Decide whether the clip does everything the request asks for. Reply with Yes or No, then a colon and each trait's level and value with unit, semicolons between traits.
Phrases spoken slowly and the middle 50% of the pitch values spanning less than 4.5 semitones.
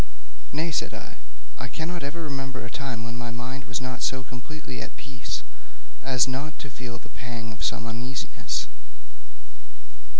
No: average, 155 wpm; average, 2.8 semitones